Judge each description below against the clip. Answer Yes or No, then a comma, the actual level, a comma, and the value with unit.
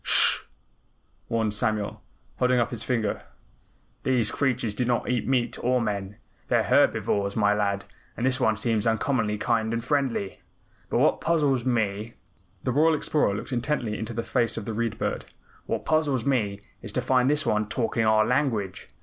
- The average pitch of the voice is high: No, low, 115 Hz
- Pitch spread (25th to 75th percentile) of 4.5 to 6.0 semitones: No, average, 3.2 semitones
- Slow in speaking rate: No, average, 175 wpm